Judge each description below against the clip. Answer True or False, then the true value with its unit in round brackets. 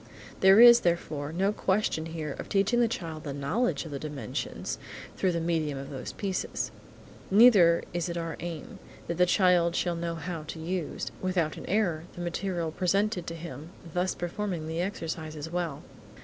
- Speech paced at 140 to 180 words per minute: True (175 wpm)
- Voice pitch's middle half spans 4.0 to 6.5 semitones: False (2.8 semitones)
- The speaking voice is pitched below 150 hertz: False (170 Hz)